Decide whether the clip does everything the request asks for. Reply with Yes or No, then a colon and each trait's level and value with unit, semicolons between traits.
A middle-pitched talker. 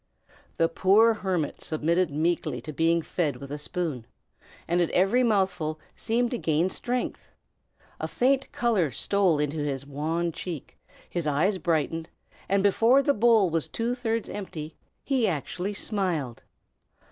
Yes: medium, 175 Hz